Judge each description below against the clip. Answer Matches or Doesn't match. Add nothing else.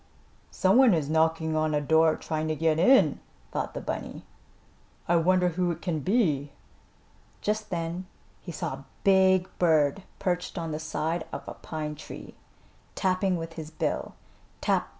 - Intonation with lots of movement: Doesn't match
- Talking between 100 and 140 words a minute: Doesn't match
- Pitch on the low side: Doesn't match